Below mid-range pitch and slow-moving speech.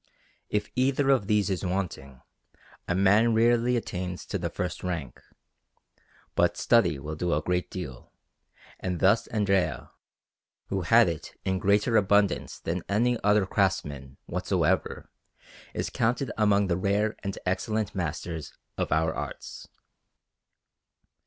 Yes: very low, 95 Hz; slow, 130 wpm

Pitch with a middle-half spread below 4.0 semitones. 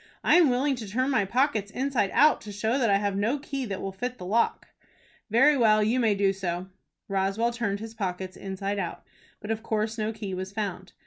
Yes: average, 3.6 semitones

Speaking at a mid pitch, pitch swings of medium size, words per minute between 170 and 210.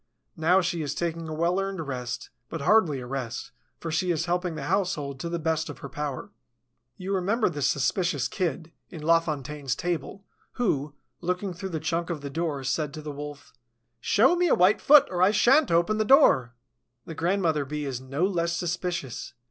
Yes: medium, 165 Hz; average, 4.0 semitones; average, 195 wpm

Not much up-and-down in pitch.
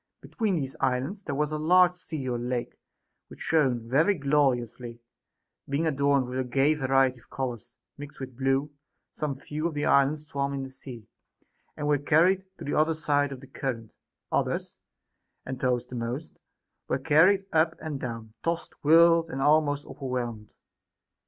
No: average, 3.3 semitones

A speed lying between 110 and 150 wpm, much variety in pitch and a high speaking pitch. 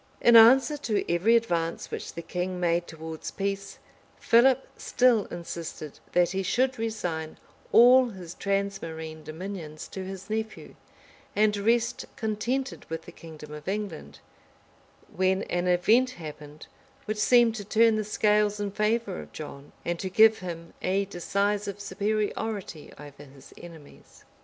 No: average, 140 wpm; average, 4.7 semitones; high, 195 Hz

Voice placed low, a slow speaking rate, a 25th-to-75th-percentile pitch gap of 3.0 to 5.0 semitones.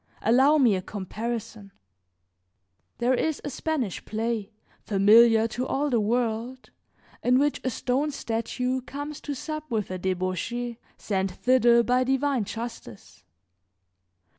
No: high, 235 Hz; slow, 125 wpm; average, 3.4 semitones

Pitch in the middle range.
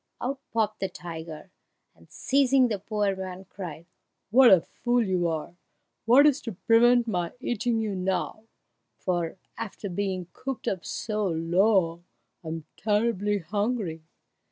No: high, 200 Hz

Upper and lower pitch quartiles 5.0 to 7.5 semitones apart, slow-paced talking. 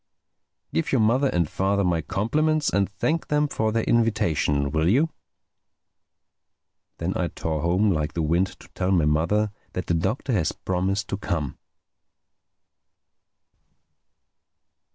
Yes: wide, 5.5 semitones; slow, 130 wpm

